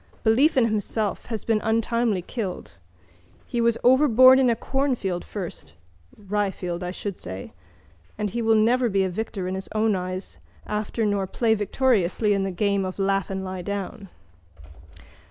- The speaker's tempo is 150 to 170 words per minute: Yes, average, 155 wpm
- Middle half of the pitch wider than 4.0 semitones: No, average, 3.3 semitones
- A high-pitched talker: Yes, high, 210 Hz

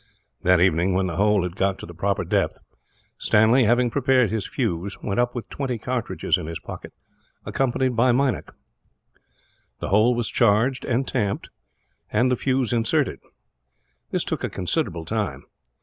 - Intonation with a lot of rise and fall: No, average, 4.4 semitones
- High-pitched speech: No, low, 110 Hz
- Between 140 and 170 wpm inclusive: Yes, average, 160 wpm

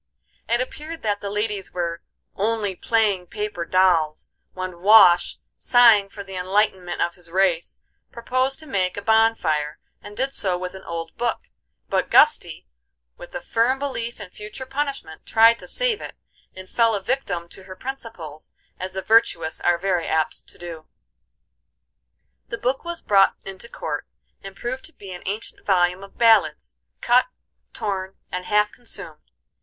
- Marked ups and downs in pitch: No, average, 4.2 semitones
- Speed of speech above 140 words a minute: Yes, average, 160 wpm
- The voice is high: Yes, high, 200 Hz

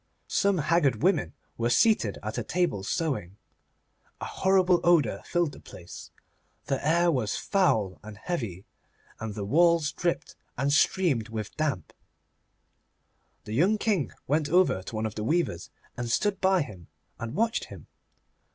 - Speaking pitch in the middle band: Yes, medium, 145 Hz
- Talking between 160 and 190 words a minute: No, average, 150 wpm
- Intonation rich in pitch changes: Yes, wide, 8.4 semitones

